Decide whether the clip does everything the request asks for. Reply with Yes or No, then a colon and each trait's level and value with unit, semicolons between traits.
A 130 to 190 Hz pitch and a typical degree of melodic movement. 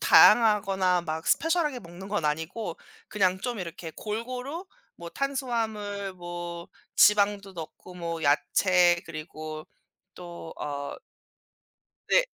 Yes: medium, 185 Hz; average, 4.2 semitones